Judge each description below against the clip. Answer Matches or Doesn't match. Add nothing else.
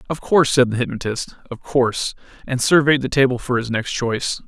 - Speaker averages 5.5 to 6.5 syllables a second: Matches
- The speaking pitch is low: Matches